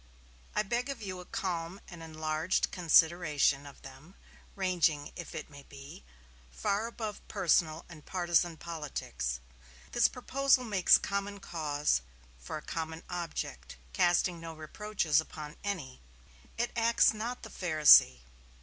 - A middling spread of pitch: Yes, average, 4.6 semitones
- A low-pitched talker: No, medium, 170 Hz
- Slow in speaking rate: Yes, slow, 130 wpm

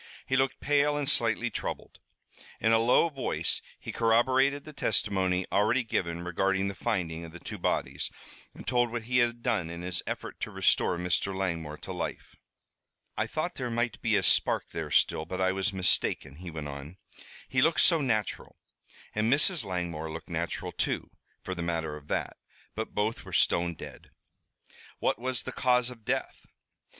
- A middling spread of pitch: No, wide, 6.2 semitones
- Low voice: Yes, low, 105 Hz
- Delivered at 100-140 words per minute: No, average, 180 wpm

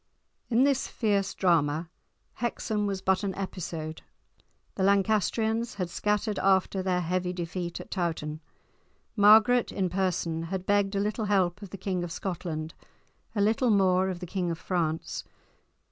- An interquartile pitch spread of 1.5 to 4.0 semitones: Yes, average, 2.8 semitones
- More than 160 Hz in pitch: Yes, high, 190 Hz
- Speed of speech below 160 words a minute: Yes, average, 150 wpm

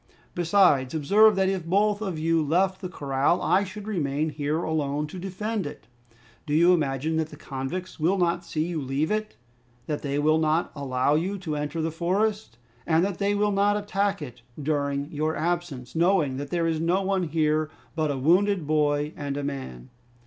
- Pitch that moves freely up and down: No, average, 4.4 semitones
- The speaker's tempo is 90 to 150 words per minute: No, average, 190 wpm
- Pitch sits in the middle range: Yes, medium, 160 Hz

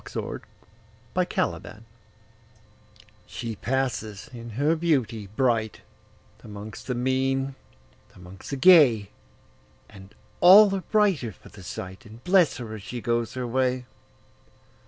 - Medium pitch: No, low, 120 Hz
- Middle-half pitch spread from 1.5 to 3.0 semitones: No, average, 3.8 semitones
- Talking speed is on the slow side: Yes, slow, 110 wpm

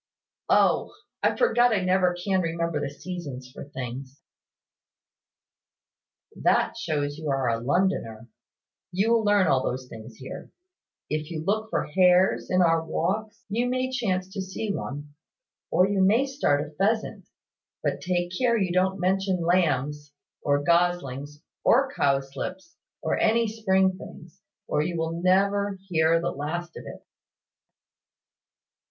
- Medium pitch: Yes, medium, 175 Hz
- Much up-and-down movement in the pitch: No, average, 5.0 semitones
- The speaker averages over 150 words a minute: No, average, 140 wpm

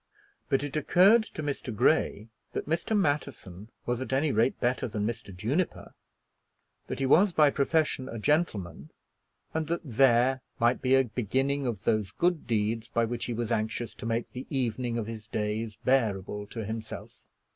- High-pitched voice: No, low, 120 Hz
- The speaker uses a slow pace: No, average, 170 wpm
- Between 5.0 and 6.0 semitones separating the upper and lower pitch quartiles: No, average, 4.3 semitones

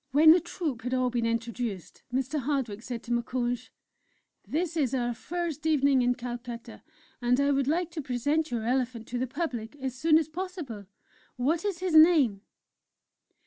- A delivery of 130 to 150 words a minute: No, average, 170 wpm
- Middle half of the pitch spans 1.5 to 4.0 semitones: No, average, 4.6 semitones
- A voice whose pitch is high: Yes, very high, 260 Hz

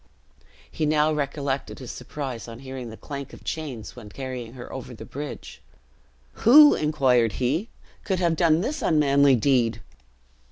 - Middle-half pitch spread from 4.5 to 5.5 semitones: No, average, 3.7 semitones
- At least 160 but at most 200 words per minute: No, average, 150 wpm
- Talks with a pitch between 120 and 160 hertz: Yes, medium, 140 Hz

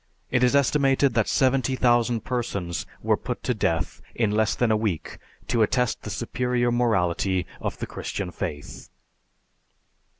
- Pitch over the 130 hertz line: No, low, 115 Hz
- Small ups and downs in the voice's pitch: No, average, 4.1 semitones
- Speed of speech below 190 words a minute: Yes, average, 140 wpm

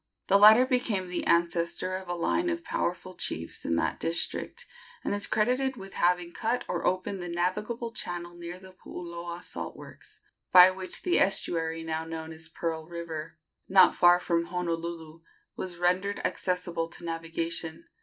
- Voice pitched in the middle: Yes, medium, 175 Hz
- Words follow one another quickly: No, average, 160 wpm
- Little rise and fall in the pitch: Yes, narrow, 2.1 semitones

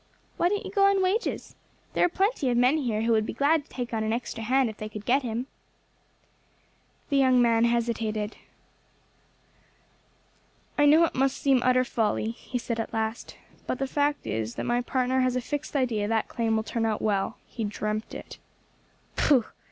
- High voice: Yes, high, 245 Hz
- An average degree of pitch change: Yes, average, 3.6 semitones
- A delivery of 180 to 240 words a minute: Yes, average, 190 wpm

